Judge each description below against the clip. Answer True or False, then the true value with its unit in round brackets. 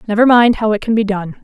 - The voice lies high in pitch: True (215 Hz)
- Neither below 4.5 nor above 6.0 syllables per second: False (6.3 syllables/s)